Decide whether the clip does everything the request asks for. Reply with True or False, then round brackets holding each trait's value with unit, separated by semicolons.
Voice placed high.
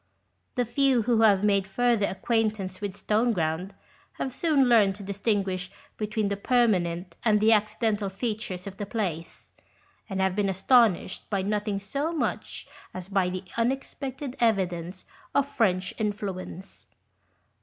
True (205 Hz)